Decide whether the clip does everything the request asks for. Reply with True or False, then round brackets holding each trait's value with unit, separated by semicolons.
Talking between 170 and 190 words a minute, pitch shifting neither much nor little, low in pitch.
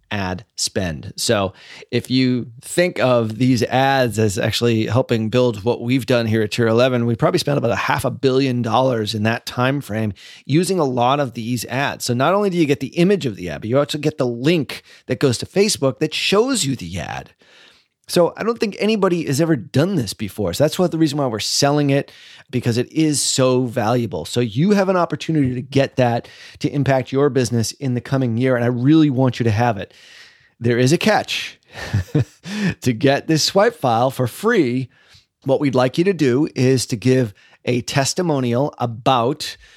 False (205 wpm; 3.6 semitones; 130 Hz)